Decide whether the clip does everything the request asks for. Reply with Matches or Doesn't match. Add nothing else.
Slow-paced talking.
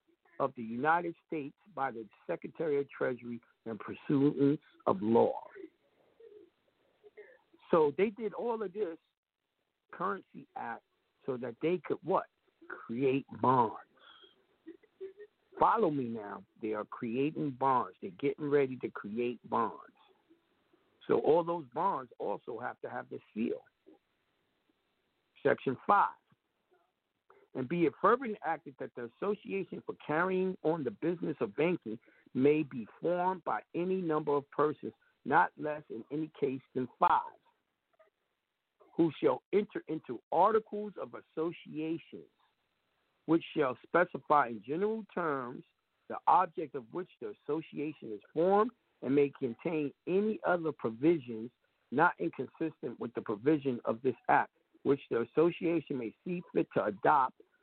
Matches